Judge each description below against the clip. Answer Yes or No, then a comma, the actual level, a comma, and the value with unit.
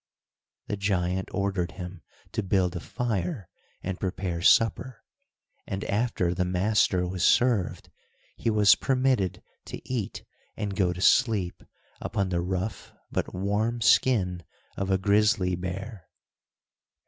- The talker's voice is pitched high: No, very low, 95 Hz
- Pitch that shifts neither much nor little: Yes, average, 3.1 semitones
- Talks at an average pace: No, slow, 125 wpm